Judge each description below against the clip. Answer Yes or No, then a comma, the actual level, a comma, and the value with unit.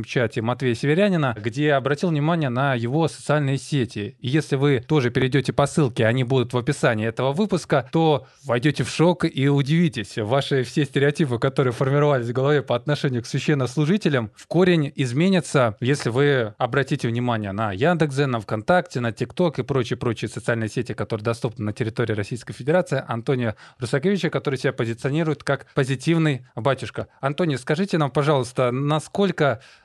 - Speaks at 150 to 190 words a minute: Yes, average, 155 wpm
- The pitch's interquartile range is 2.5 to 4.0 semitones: Yes, average, 3.7 semitones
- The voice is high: No, medium, 140 Hz